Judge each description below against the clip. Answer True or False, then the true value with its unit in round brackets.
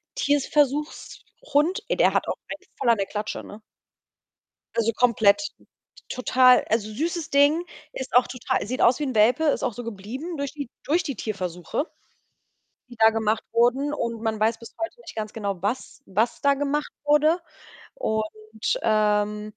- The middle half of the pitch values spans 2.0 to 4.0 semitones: False (5.1 semitones)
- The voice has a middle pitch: False (240 Hz)